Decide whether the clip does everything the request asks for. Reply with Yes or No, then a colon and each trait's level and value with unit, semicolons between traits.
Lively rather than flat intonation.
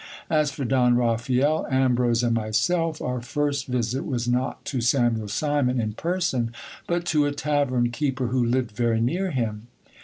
No: average, 3.5 semitones